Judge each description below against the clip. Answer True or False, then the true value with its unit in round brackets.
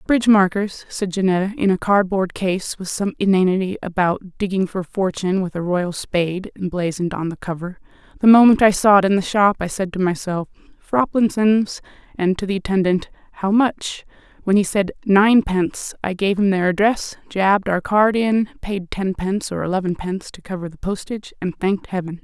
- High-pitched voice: True (195 Hz)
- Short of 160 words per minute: False (180 wpm)